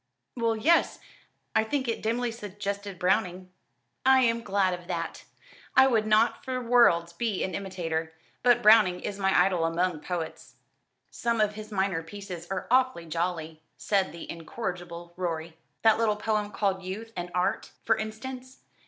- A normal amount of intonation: Yes, average, 4.2 semitones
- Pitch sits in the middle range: No, high, 200 Hz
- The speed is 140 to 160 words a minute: Yes, average, 155 wpm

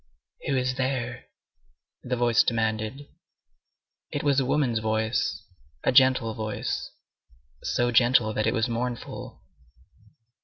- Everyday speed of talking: No, slow, 115 wpm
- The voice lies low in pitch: Yes, low, 120 Hz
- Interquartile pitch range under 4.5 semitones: Yes, narrow, 2.5 semitones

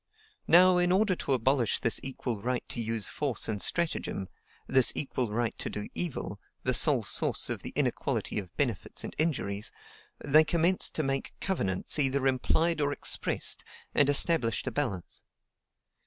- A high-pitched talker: No, low, 135 Hz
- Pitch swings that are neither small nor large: No, wide, 5.7 semitones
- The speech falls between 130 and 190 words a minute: Yes, average, 155 wpm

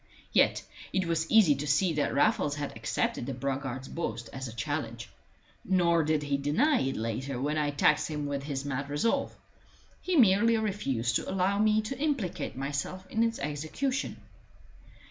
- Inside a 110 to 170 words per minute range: Yes, average, 165 wpm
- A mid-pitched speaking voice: Yes, medium, 150 Hz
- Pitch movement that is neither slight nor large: No, wide, 5.7 semitones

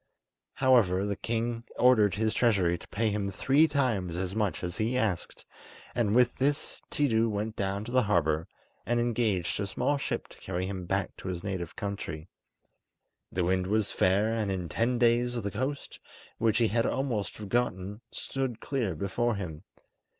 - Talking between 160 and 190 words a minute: Yes, average, 170 wpm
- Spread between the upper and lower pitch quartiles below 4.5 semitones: Yes, average, 4.1 semitones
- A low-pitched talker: Yes, low, 105 Hz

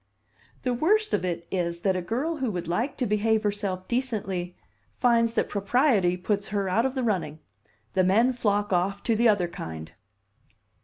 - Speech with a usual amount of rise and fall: Yes, average, 4.7 semitones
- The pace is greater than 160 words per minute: Yes, average, 175 wpm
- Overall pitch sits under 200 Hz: No, high, 205 Hz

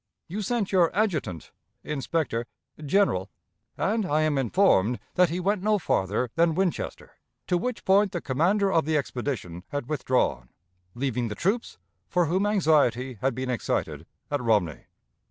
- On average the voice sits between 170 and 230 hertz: No, medium, 155 Hz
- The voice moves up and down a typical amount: No, wide, 7.4 semitones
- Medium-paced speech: Yes, average, 150 wpm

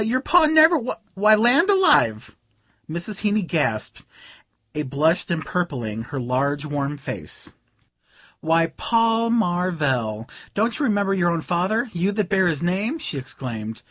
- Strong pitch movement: Yes, wide, 7.5 semitones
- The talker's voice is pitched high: No, medium, 175 Hz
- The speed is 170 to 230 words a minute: No, average, 140 wpm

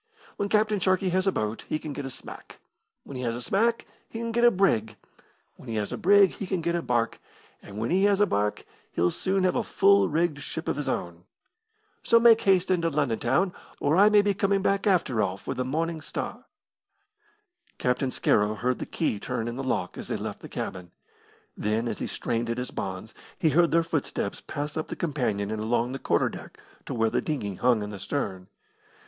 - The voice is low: No, medium, 145 Hz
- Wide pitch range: Yes, wide, 8.9 semitones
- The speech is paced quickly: Yes, fast, 220 wpm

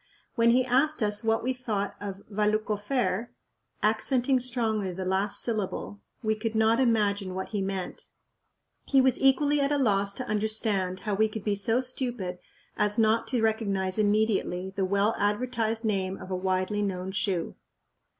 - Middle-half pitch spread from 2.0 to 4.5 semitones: Yes, average, 3.0 semitones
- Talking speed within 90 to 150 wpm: No, average, 165 wpm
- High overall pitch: Yes, high, 215 Hz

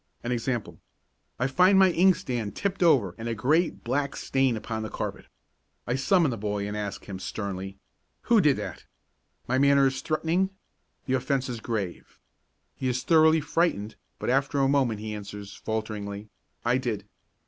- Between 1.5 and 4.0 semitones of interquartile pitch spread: No, average, 5.1 semitones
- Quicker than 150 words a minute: Yes, average, 165 wpm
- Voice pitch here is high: No, low, 125 Hz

